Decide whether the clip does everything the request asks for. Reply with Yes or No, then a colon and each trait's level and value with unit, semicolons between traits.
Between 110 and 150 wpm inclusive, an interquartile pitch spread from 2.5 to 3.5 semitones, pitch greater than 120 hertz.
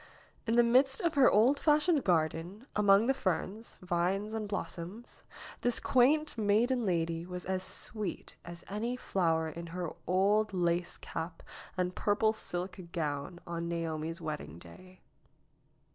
No: average, 140 wpm; average, 4.7 semitones; medium, 185 Hz